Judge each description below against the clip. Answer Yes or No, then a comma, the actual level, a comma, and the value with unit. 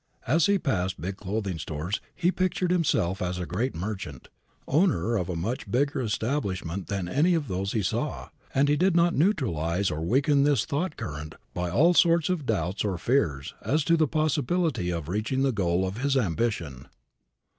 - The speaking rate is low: No, average, 180 wpm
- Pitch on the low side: Yes, low, 110 Hz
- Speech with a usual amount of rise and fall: No, wide, 8.8 semitones